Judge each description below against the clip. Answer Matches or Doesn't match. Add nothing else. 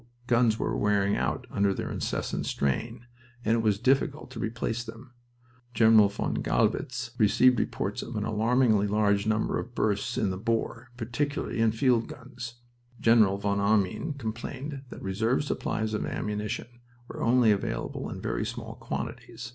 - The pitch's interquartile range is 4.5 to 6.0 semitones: Doesn't match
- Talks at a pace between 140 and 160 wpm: Matches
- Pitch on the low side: Matches